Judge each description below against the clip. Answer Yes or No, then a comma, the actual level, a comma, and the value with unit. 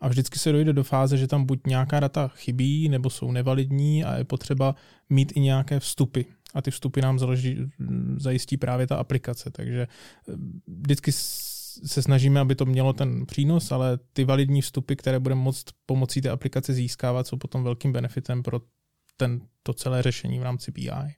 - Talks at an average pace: No, fast, 175 wpm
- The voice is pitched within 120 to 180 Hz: Yes, low, 135 Hz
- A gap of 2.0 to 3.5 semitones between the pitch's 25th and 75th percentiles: No, narrow, 1.6 semitones